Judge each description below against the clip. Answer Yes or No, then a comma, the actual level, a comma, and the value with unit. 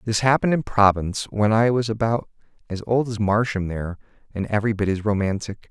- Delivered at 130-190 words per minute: Yes, average, 180 wpm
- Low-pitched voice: Yes, low, 105 Hz